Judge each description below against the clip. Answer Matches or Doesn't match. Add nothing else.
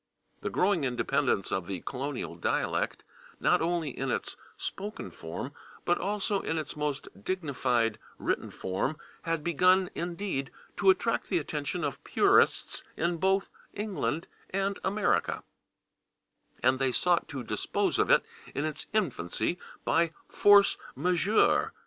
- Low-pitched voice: Doesn't match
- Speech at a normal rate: Doesn't match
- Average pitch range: Doesn't match